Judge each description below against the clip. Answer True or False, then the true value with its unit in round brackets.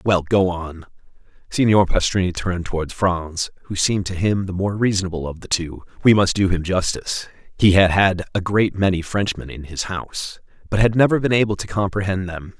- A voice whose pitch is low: True (95 Hz)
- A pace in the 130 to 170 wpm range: False (190 wpm)